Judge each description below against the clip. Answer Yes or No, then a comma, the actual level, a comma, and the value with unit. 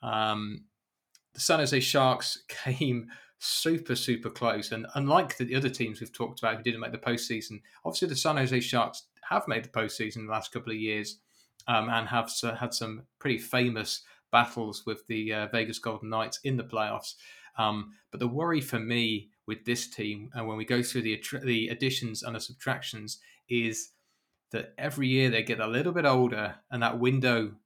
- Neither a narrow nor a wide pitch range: No, narrow, 2.3 semitones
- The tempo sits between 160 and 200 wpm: Yes, average, 190 wpm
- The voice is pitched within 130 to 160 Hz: No, low, 115 Hz